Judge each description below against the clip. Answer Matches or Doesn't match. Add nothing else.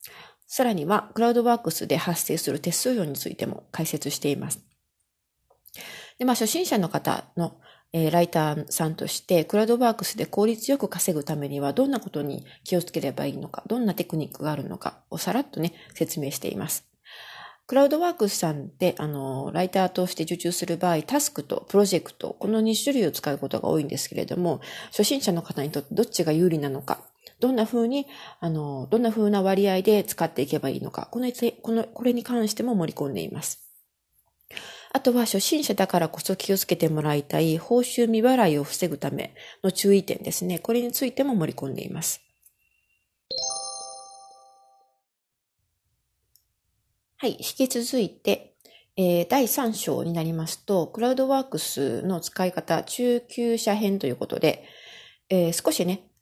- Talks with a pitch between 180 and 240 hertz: Matches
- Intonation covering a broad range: Matches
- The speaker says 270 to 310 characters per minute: Doesn't match